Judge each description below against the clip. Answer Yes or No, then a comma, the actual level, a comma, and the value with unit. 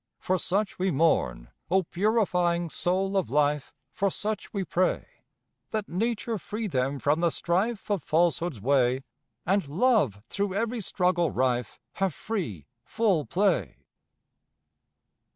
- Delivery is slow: Yes, slow, 130 wpm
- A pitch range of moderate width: No, wide, 5.7 semitones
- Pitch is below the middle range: No, medium, 180 Hz